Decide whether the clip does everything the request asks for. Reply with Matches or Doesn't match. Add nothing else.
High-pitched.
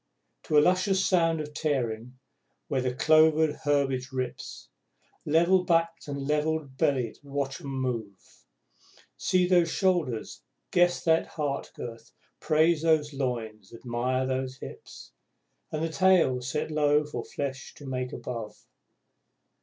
Doesn't match